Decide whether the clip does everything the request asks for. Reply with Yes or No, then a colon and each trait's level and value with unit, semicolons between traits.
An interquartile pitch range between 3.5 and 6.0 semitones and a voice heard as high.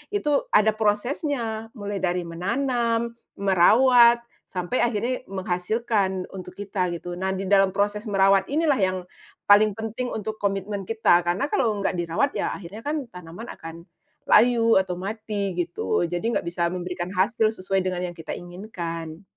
Yes: average, 3.9 semitones; high, 200 Hz